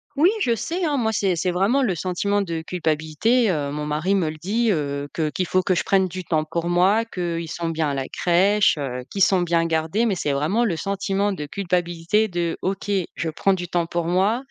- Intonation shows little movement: No, average, 3.6 semitones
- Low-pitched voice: No, medium, 180 Hz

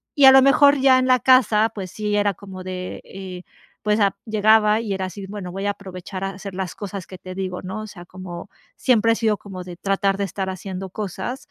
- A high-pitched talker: Yes, high, 200 Hz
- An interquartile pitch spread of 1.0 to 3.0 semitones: Yes, narrow, 2.6 semitones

